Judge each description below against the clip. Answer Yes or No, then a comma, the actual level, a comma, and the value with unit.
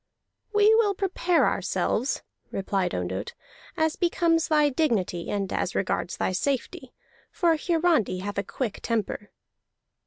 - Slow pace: Yes, slow, 125 wpm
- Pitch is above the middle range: Yes, very high, 280 Hz